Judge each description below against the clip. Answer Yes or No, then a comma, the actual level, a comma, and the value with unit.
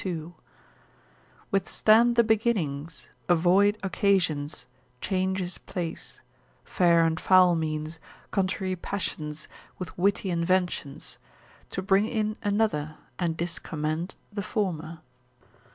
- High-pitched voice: No, medium, 180 Hz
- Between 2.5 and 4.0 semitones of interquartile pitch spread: Yes, average, 3.6 semitones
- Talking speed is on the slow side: Yes, slow, 95 wpm